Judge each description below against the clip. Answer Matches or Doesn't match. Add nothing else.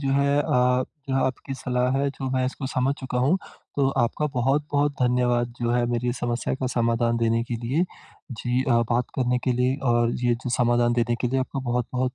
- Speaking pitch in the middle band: Doesn't match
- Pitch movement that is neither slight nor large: Doesn't match